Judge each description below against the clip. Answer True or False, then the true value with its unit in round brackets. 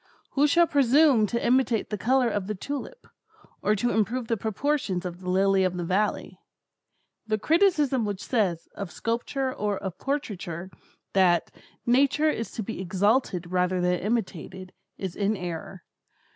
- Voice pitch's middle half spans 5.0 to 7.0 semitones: True (5.6 semitones)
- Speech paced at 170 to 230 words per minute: False (155 wpm)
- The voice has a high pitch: True (210 Hz)